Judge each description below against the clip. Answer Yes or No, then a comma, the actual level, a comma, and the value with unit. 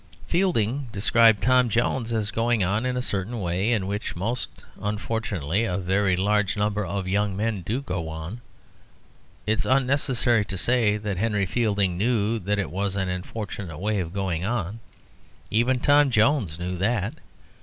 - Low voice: Yes, low, 105 Hz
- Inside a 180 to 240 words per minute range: No, average, 165 wpm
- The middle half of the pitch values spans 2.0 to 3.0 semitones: No, average, 3.6 semitones